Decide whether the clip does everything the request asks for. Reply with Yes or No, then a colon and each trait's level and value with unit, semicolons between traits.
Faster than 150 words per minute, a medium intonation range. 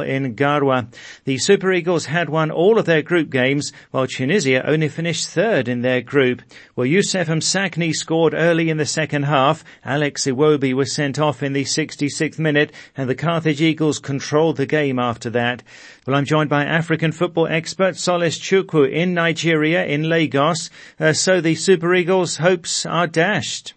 Yes: average, 170 wpm; average, 3.3 semitones